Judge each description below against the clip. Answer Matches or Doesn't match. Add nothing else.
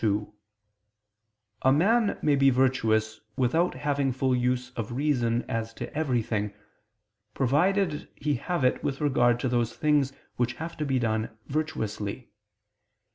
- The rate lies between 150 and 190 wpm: Doesn't match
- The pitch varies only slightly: Doesn't match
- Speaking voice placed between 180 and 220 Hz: Doesn't match